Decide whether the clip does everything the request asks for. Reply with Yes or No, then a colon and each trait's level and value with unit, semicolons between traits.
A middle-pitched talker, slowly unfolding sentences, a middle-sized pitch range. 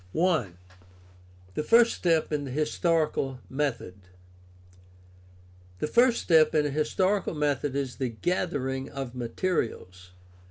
Yes: medium, 145 Hz; slow, 115 wpm; average, 4.4 semitones